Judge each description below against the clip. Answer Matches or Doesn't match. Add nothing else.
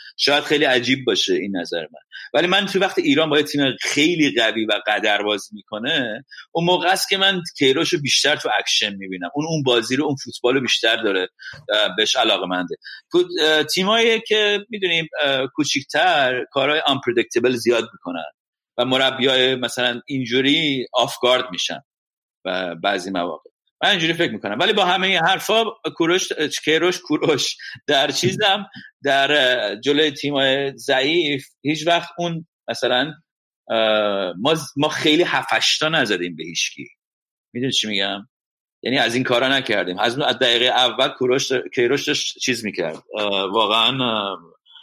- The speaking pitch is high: Doesn't match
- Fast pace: Doesn't match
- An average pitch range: Doesn't match